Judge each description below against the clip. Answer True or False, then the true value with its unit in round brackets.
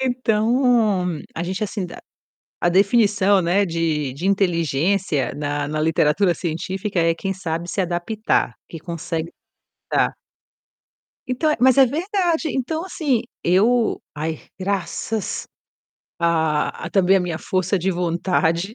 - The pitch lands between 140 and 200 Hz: True (185 Hz)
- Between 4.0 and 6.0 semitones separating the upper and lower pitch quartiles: True (4.7 semitones)